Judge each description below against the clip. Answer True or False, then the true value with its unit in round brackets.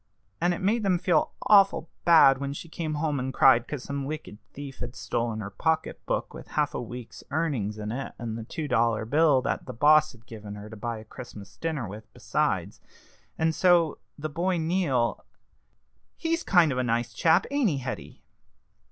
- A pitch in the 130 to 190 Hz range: True (140 Hz)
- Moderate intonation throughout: False (5.8 semitones)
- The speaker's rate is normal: True (195 wpm)